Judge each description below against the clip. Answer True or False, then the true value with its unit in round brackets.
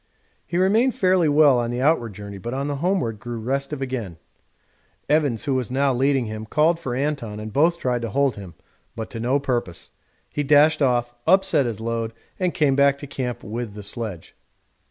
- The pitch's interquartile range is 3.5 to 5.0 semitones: True (4.3 semitones)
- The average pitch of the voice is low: True (130 Hz)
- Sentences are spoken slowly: False (195 wpm)